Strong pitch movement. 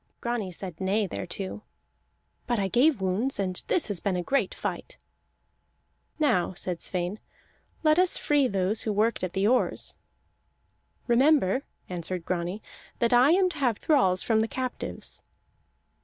Yes: wide, 5.7 semitones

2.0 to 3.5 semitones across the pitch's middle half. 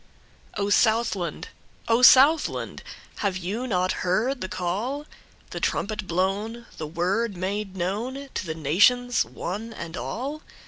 No: average, 4.7 semitones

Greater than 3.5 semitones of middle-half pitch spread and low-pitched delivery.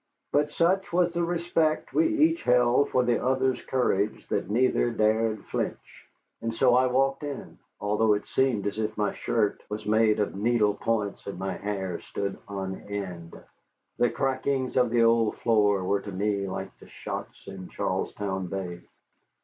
Yes: average, 4.3 semitones; low, 110 Hz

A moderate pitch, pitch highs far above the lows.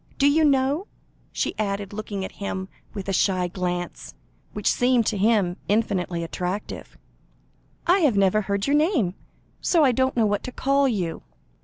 No: high, 210 Hz; wide, 5.7 semitones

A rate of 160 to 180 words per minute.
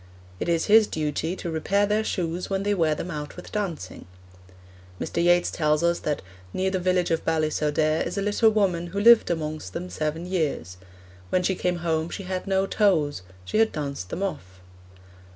No: average, 190 wpm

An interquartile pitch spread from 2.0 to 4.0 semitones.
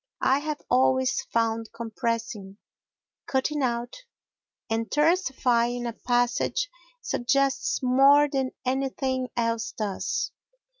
Yes: narrow, 2.6 semitones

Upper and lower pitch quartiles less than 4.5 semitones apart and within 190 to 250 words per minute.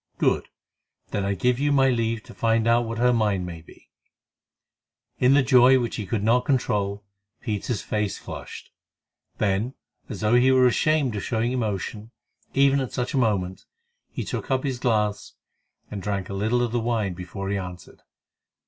No: average, 3.5 semitones; average, 175 wpm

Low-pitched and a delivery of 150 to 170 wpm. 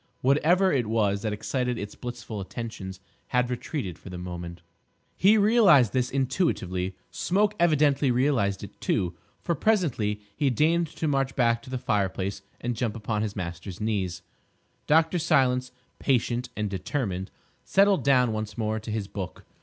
Yes: low, 120 Hz; average, 155 wpm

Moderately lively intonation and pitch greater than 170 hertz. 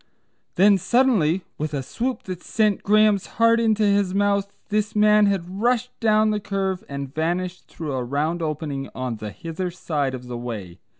No: wide, 6.2 semitones; medium, 185 Hz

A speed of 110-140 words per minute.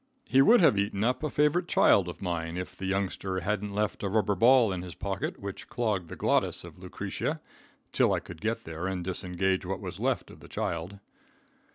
No: fast, 205 wpm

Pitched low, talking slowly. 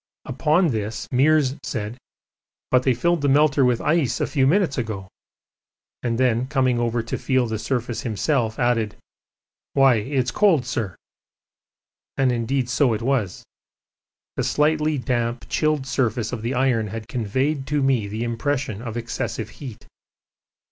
No: low, 125 Hz; average, 150 wpm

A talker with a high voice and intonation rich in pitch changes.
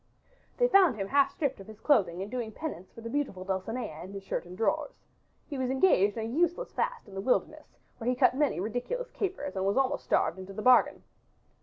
Yes: high, 245 Hz; wide, 6.6 semitones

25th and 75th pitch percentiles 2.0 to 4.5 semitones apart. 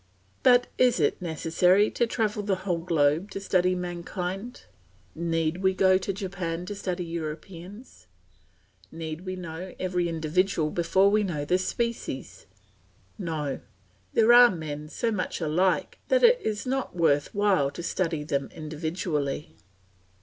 Yes: average, 3.6 semitones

